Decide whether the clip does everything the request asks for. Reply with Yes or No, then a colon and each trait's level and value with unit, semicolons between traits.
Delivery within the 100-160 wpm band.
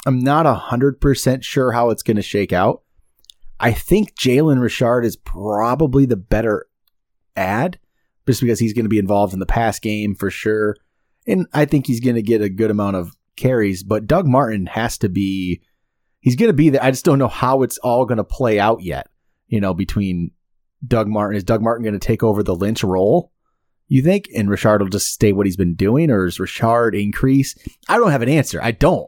No: fast, 205 wpm